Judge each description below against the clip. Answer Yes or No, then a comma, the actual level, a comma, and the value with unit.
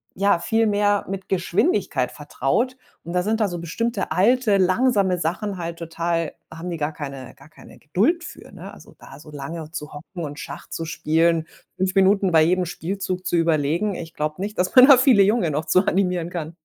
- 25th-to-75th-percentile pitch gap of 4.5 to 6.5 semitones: No, average, 3.8 semitones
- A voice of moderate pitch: Yes, medium, 180 Hz